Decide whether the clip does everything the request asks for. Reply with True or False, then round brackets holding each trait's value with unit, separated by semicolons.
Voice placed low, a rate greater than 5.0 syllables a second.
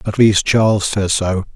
False (100 Hz; 4.4 syllables/s)